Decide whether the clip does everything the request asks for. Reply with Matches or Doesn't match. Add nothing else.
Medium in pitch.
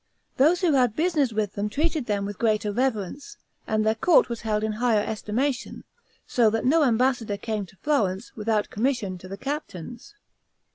Doesn't match